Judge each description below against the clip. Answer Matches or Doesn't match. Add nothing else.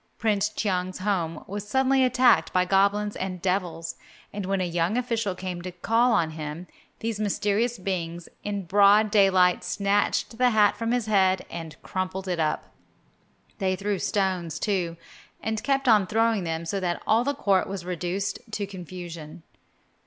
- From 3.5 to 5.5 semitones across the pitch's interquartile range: Doesn't match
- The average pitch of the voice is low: Doesn't match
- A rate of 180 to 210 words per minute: Doesn't match